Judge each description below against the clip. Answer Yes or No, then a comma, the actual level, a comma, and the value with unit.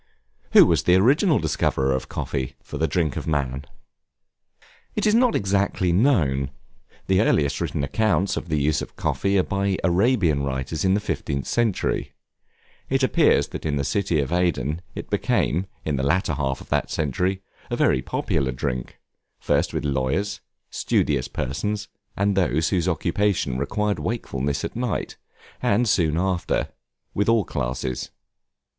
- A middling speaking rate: Yes, average, 155 wpm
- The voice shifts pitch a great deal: Yes, wide, 6.2 semitones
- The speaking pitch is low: Yes, very low, 85 Hz